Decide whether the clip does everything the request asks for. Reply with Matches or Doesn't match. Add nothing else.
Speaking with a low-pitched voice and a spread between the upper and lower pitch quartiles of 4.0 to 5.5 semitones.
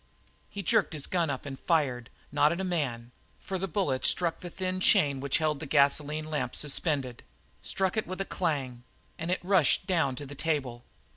Doesn't match